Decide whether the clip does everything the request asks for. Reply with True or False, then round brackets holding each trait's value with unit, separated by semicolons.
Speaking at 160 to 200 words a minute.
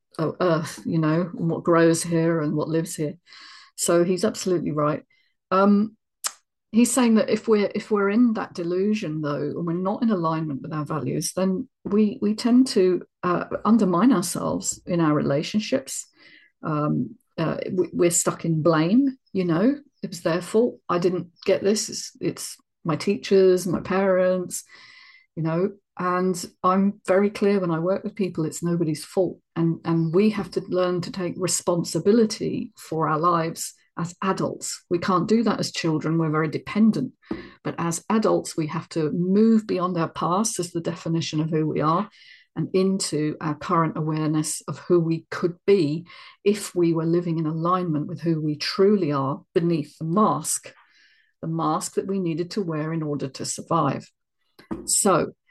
True (175 wpm)